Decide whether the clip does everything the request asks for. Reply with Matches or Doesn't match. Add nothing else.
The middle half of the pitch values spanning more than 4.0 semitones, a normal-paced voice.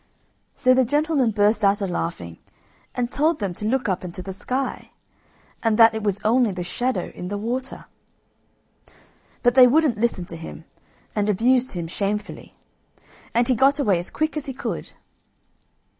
Matches